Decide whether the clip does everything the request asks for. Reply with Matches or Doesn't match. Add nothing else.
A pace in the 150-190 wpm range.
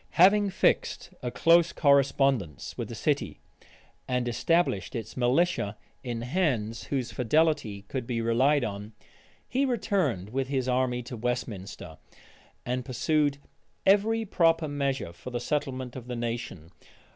Doesn't match